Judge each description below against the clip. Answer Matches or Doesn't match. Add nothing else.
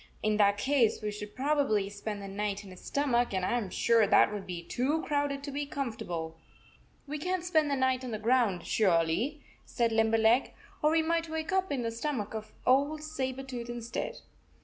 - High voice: Matches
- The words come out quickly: Matches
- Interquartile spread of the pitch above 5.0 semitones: Matches